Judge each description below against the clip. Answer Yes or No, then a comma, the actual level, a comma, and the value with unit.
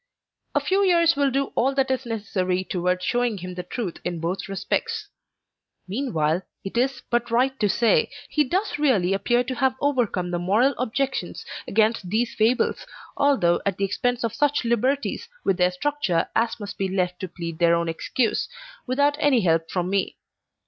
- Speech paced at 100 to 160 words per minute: No, average, 175 wpm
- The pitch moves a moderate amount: No, wide, 6.5 semitones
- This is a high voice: Yes, high, 225 Hz